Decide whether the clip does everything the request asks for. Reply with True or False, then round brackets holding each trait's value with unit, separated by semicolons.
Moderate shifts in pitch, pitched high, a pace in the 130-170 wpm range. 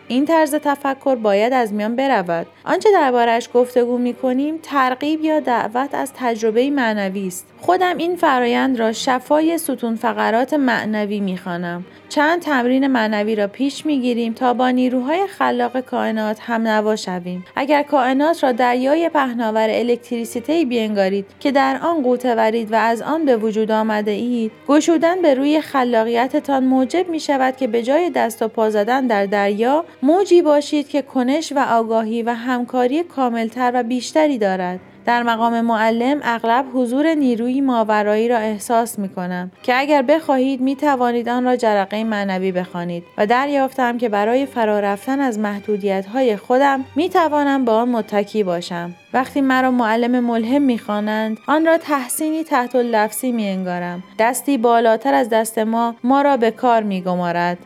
True (4.0 semitones; 245 Hz; 150 wpm)